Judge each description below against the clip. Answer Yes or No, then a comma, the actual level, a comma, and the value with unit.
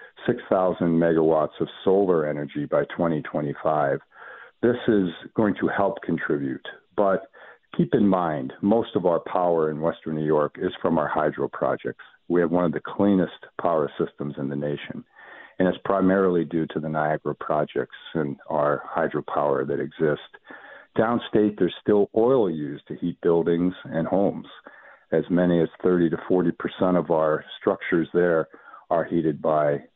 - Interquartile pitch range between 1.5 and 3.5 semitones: Yes, narrow, 2.5 semitones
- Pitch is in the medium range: No, very low, 85 Hz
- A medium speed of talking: Yes, average, 155 wpm